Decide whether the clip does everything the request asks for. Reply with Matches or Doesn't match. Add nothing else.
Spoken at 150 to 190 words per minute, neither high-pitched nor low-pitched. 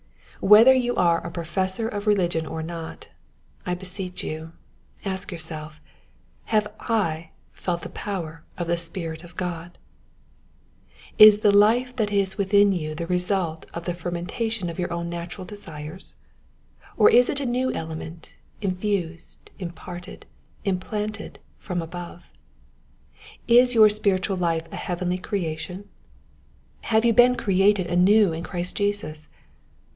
Doesn't match